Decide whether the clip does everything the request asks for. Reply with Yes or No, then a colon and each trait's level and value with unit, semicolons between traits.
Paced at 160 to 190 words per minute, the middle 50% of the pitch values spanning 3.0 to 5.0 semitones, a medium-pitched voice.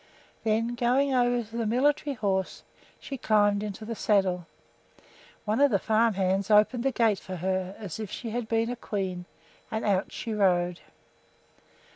No: average, 165 wpm; average, 3.6 semitones; high, 215 Hz